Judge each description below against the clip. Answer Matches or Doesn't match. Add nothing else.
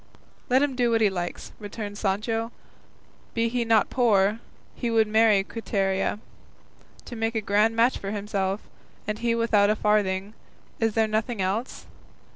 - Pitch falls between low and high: Doesn't match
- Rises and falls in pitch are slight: Matches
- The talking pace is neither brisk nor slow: Matches